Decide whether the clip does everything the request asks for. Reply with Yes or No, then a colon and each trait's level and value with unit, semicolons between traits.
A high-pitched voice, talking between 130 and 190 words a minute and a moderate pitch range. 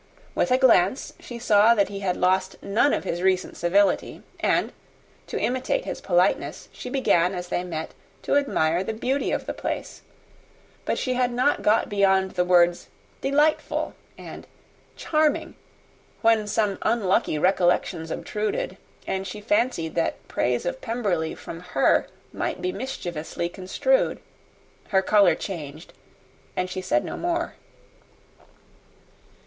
No: high, 195 Hz; average, 140 wpm; wide, 5.9 semitones